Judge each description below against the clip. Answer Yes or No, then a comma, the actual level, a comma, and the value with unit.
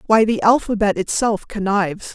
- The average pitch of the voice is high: Yes, high, 205 Hz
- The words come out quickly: No, average, 140 wpm